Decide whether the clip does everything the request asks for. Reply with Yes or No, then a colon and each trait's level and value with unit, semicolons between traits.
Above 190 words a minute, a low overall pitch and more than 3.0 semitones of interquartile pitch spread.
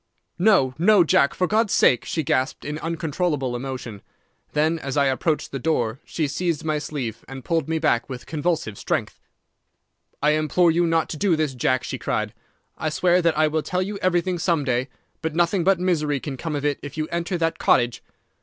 No: average, 200 wpm; medium, 155 Hz; average, 3.9 semitones